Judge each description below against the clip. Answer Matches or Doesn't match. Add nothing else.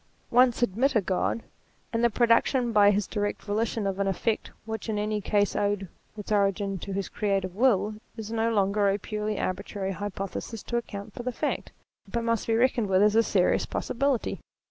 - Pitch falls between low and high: Doesn't match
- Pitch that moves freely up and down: Doesn't match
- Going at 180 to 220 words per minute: Matches